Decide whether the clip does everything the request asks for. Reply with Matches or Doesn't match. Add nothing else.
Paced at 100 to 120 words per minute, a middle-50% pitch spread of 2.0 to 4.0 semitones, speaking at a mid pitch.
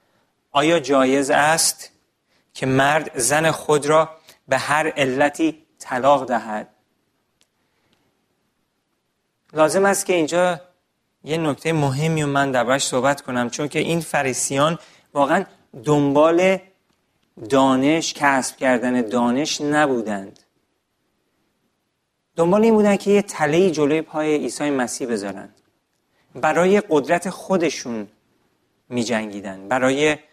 Matches